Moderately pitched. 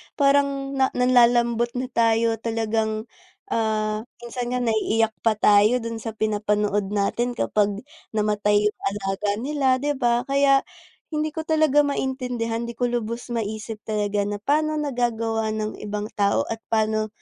No: high, 225 Hz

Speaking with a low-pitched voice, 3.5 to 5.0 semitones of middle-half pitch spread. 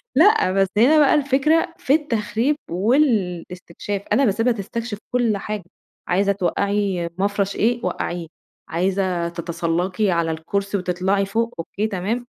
No: high, 200 Hz; average, 4.6 semitones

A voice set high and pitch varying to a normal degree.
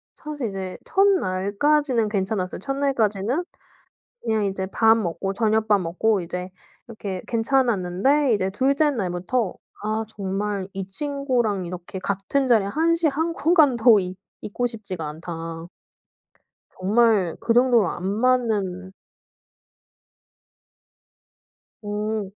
Yes: high, 215 Hz; average, 5.0 semitones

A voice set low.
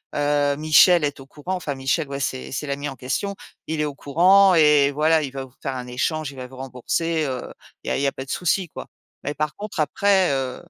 No: medium, 145 Hz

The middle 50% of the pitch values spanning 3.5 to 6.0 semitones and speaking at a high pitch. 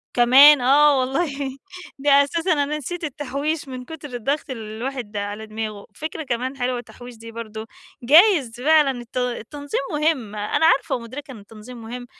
Yes: average, 4.0 semitones; very high, 255 Hz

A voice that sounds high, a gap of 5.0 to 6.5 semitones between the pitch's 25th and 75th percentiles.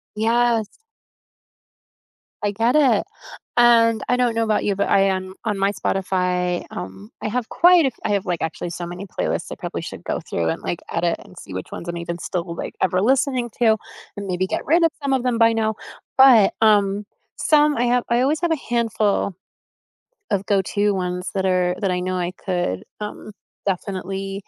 No: high, 200 Hz; average, 4.5 semitones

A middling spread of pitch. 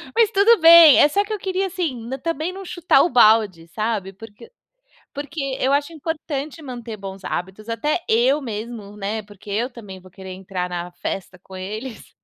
No: wide, 8.0 semitones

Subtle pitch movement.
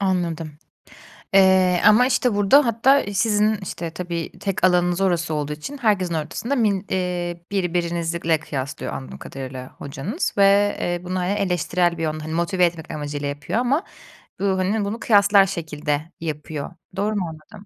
No: average, 4.0 semitones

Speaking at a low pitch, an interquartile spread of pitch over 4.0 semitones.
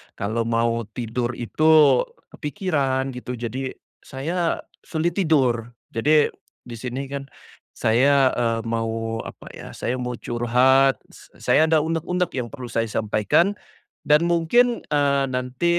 Yes: low, 130 Hz; average, 4.8 semitones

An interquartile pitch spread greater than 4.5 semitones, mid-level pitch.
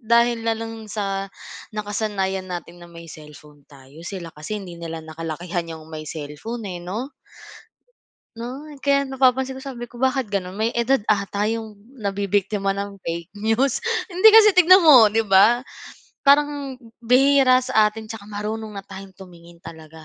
No: wide, 5.6 semitones; high, 210 Hz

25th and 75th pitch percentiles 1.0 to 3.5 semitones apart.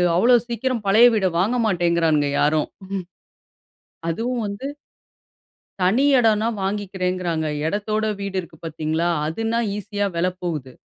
No: average, 4.7 semitones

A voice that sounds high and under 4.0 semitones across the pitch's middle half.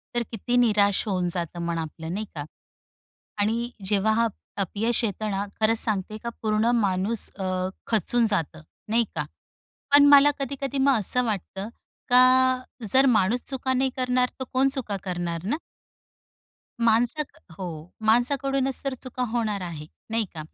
No: high, 225 Hz; average, 4.5 semitones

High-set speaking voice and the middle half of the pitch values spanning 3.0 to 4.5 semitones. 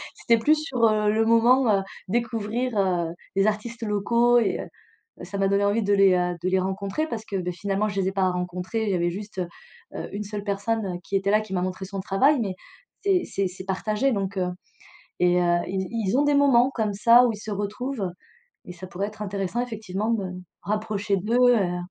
Yes: high, 205 Hz; average, 3.3 semitones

